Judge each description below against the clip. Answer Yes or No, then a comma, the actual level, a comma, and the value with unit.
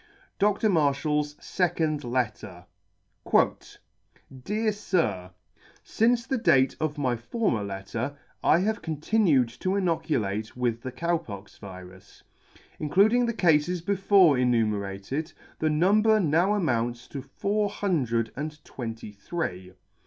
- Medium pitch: Yes, medium, 150 Hz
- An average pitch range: No, wide, 8.4 semitones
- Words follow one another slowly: Yes, slow, 115 wpm